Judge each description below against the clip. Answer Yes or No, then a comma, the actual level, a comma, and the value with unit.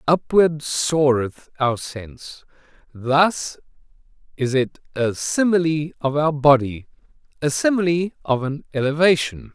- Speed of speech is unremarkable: No, slow, 105 wpm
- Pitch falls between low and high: Yes, medium, 145 Hz